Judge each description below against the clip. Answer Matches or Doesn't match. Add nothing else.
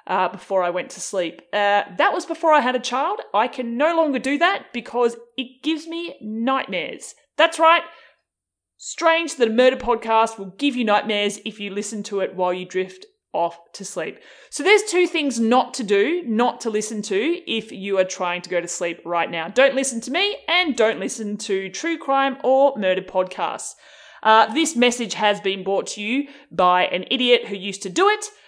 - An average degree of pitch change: Doesn't match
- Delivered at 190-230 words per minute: Matches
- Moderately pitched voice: Doesn't match